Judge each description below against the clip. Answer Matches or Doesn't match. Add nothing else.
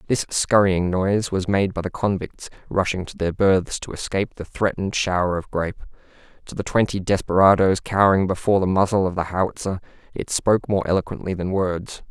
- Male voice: Matches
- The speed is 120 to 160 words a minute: Doesn't match